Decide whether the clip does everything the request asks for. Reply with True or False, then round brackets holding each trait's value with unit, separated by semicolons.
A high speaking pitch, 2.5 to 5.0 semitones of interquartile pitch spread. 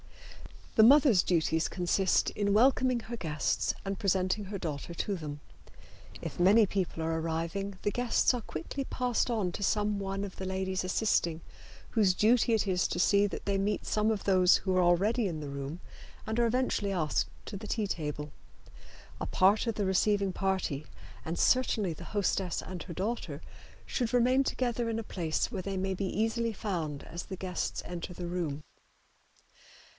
True (195 Hz; 3.8 semitones)